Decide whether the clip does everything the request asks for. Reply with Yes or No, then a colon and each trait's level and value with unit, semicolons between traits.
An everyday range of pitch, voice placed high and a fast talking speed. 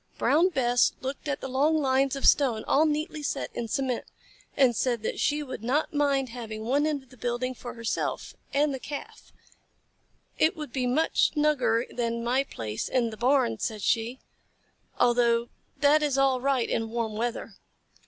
No: average, 3.3 semitones; very high, 260 Hz; average, 175 wpm